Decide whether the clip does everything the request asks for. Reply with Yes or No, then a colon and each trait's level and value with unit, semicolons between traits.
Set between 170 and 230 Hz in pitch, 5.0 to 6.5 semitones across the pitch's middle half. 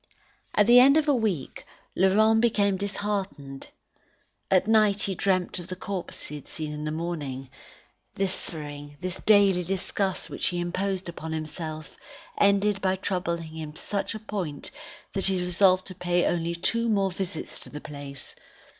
No: medium, 185 Hz; average, 4.0 semitones